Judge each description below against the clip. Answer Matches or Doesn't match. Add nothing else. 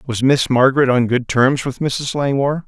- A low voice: Matches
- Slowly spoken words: Doesn't match